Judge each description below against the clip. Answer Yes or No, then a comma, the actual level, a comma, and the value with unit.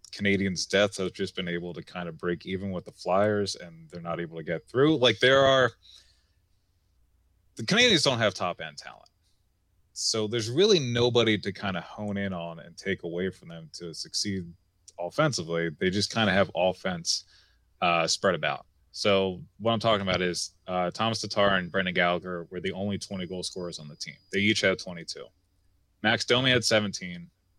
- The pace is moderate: Yes, average, 190 wpm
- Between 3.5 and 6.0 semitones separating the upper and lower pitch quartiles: No, average, 2.9 semitones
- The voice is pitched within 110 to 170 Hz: No, very low, 95 Hz